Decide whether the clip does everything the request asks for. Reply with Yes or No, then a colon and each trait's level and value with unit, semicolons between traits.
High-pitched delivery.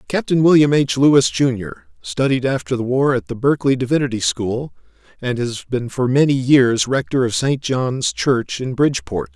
No: low, 125 Hz